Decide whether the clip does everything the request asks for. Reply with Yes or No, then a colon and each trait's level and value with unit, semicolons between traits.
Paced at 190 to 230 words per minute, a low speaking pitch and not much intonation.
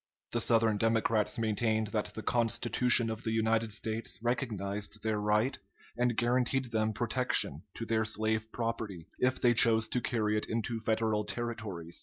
No: average, 155 wpm; low, 110 Hz; narrow, 1.6 semitones